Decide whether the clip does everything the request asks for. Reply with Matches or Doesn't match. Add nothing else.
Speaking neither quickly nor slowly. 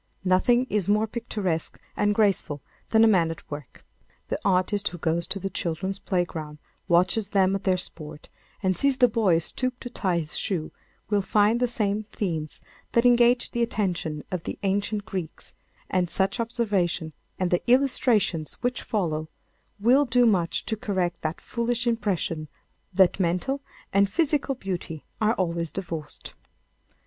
Matches